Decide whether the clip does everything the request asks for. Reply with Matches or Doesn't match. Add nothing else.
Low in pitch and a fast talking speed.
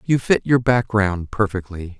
Doesn't match